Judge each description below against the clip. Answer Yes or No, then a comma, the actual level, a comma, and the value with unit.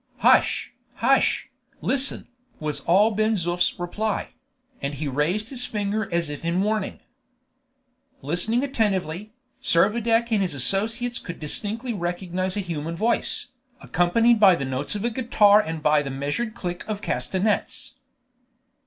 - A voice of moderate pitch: No, high, 195 Hz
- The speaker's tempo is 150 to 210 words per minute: No, slow, 135 wpm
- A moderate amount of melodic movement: Yes, average, 4.7 semitones